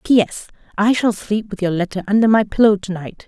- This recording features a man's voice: No, female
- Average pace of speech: No, fast, 220 wpm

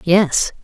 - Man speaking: No, female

